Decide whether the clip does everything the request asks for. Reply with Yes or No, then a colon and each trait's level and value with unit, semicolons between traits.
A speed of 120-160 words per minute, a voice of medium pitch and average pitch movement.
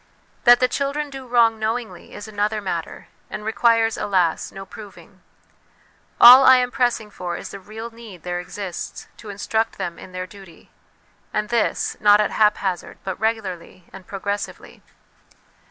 No: average, 155 wpm; high, 210 Hz; average, 3.3 semitones